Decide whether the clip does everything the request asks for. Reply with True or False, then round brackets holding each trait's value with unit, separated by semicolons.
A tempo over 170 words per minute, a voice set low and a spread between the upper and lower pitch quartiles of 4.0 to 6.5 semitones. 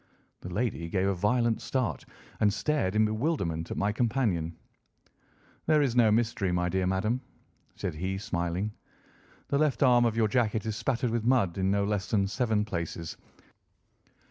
False (165 wpm; 105 Hz; 4.3 semitones)